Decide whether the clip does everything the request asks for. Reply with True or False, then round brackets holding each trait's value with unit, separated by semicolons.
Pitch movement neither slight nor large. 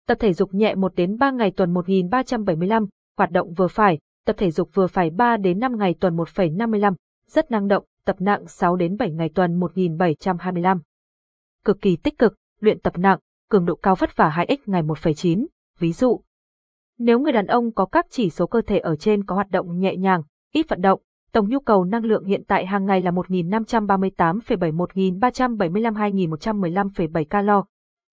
True (3.4 semitones)